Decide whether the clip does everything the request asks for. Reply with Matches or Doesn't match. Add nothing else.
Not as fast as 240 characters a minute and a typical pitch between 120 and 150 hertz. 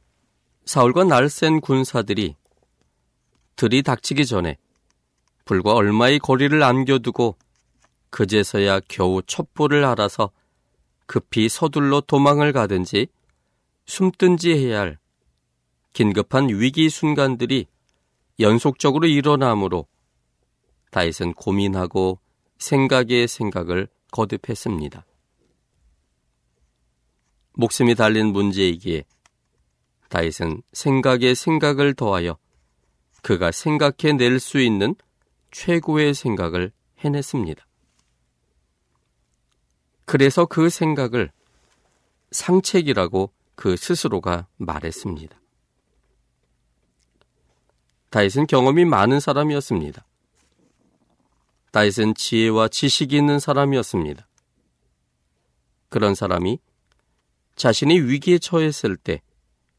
Doesn't match